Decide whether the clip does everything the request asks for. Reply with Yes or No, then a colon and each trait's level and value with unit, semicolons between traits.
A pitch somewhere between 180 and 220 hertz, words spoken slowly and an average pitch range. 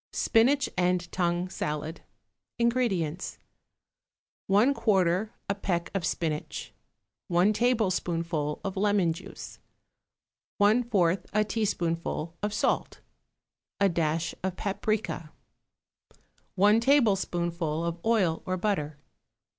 Yes: medium, 185 Hz; slow, 90 wpm; average, 3.9 semitones